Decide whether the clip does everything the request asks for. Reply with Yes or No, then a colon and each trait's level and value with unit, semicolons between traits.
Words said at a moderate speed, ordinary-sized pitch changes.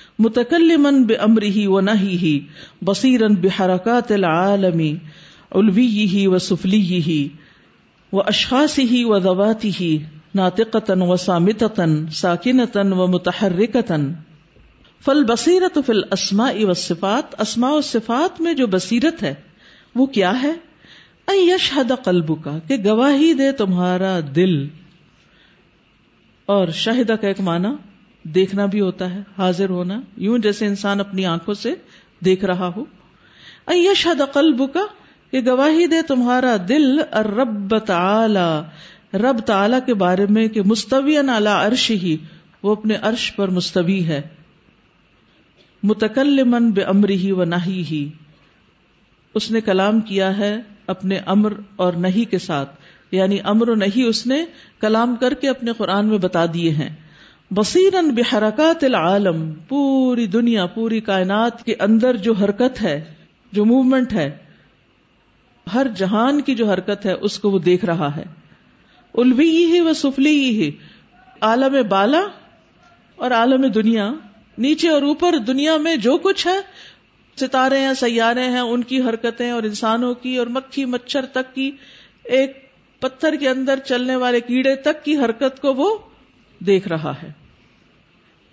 No: average, 140 wpm; wide, 5.7 semitones